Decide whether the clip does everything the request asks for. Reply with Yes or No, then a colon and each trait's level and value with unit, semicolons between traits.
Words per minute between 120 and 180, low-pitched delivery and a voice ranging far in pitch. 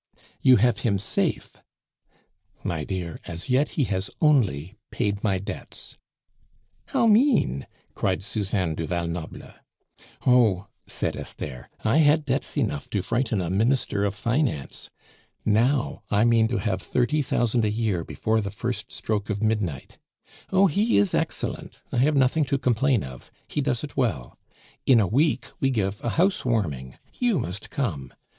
Yes: average, 160 wpm; low, 110 Hz; wide, 6.0 semitones